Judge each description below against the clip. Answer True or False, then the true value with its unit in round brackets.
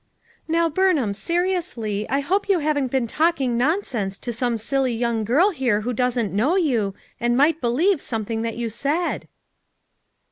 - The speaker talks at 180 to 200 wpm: False (155 wpm)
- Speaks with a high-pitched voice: True (255 Hz)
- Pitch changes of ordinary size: False (6.1 semitones)